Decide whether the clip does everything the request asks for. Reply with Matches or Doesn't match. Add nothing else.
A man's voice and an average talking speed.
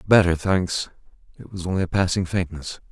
Matches